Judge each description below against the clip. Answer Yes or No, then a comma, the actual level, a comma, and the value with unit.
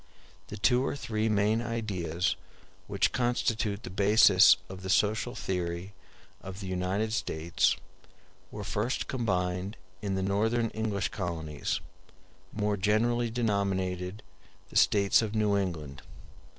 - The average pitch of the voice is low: Yes, low, 100 Hz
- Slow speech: Yes, slow, 125 wpm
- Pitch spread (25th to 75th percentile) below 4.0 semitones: Yes, average, 3.2 semitones